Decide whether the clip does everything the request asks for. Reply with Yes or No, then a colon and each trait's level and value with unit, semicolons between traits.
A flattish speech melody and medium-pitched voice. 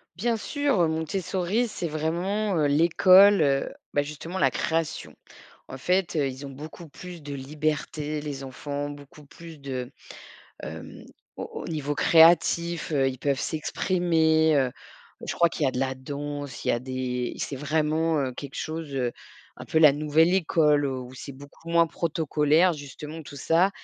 No: average, 3.0 semitones; medium, 155 Hz